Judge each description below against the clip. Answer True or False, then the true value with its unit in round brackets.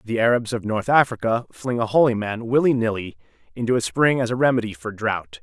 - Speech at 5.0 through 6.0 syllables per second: True (5.8 syllables/s)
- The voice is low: True (115 Hz)